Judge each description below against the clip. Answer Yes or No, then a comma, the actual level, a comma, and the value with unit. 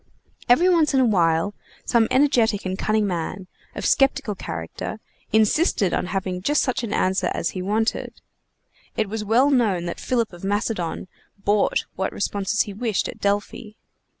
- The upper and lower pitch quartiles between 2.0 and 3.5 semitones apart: No, average, 3.9 semitones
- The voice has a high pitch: Yes, high, 210 Hz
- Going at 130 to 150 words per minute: No, average, 160 wpm